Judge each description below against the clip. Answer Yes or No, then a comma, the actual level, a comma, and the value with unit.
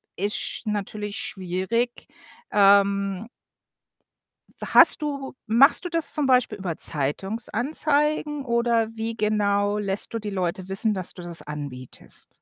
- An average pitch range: Yes, average, 3.7 semitones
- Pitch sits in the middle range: No, high, 210 Hz